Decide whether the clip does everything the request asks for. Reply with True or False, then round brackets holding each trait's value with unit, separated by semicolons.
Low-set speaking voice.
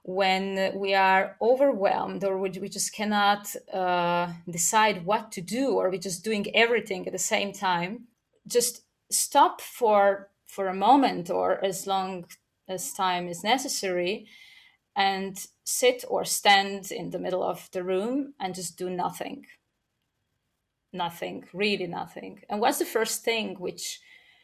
False (195 Hz)